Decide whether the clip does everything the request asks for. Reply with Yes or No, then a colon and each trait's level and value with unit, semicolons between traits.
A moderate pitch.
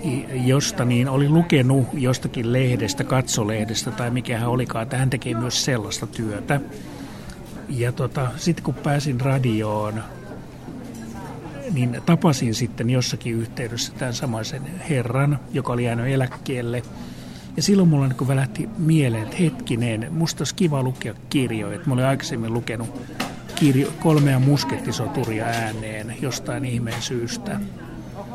No: low, 125 Hz